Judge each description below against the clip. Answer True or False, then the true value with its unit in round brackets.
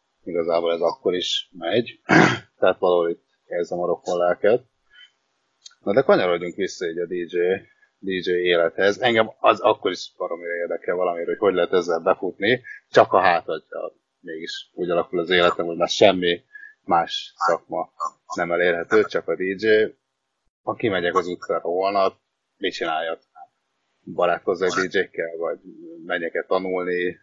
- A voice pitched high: True (400 Hz)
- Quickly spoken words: False (140 wpm)